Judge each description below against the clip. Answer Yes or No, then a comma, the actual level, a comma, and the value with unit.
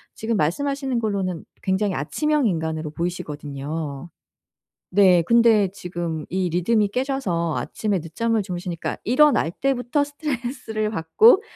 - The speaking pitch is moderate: No, high, 200 Hz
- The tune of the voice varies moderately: No, wide, 6.4 semitones